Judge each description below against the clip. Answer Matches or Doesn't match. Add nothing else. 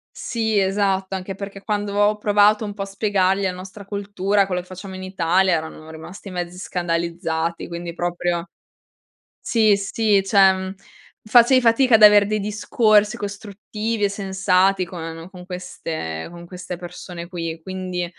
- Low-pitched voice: Doesn't match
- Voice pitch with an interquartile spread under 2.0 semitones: Doesn't match